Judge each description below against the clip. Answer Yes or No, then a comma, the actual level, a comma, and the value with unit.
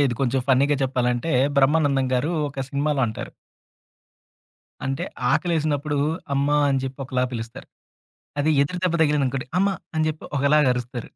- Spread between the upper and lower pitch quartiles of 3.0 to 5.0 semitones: No, narrow, 2.6 semitones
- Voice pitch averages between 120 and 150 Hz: Yes, medium, 140 Hz